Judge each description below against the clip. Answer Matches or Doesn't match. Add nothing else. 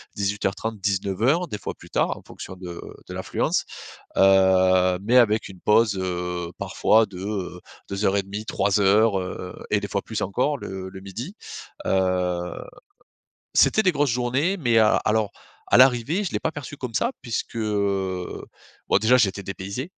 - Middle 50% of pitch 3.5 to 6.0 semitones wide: Matches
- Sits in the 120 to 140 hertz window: Doesn't match